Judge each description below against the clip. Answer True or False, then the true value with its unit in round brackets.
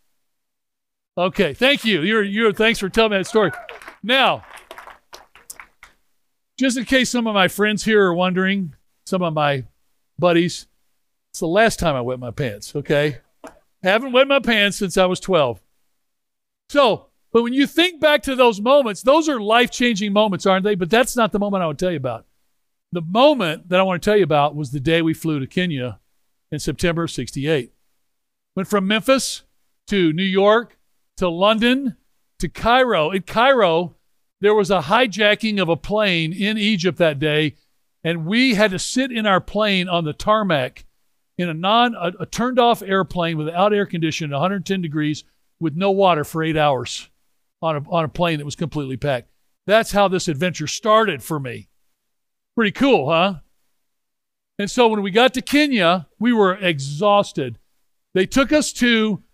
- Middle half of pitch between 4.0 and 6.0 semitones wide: True (5.3 semitones)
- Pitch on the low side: False (190 Hz)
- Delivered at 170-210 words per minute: True (180 wpm)